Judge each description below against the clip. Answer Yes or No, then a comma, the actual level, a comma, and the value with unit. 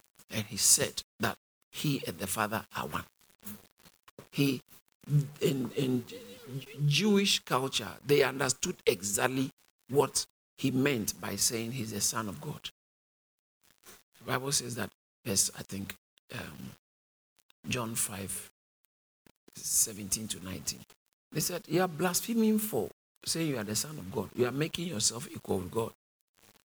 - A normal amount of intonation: No, wide, 6.1 semitones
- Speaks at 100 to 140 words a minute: Yes, slow, 135 wpm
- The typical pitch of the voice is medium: No, low, 120 Hz